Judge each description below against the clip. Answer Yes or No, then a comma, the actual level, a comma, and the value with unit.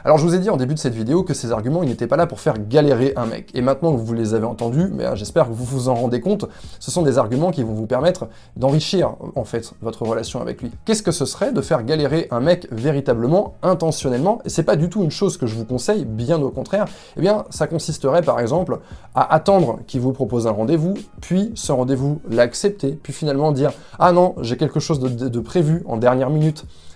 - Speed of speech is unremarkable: No, fast, 240 wpm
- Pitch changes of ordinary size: No, wide, 5.9 semitones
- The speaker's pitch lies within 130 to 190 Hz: Yes, medium, 140 Hz